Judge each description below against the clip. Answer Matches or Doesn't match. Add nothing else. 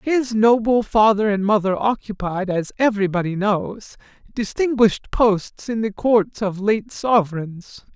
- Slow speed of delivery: Matches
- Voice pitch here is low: Doesn't match